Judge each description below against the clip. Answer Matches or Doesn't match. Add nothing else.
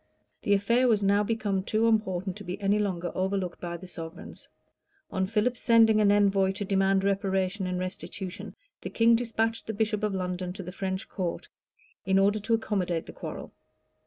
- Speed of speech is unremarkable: Matches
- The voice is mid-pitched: Doesn't match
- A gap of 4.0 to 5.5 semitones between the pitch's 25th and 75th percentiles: Doesn't match